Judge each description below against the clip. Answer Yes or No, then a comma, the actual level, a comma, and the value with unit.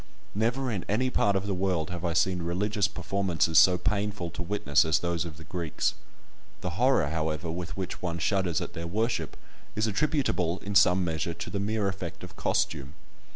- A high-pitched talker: No, very low, 90 Hz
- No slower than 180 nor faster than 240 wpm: Yes, average, 190 wpm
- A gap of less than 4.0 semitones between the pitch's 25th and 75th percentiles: Yes, average, 3.3 semitones